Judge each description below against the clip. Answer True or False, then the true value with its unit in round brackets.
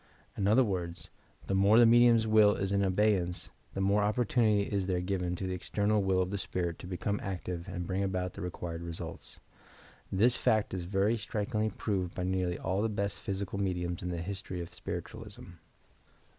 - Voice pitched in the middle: False (95 Hz)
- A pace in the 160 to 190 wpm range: True (185 wpm)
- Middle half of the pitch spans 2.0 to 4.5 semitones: True (2.4 semitones)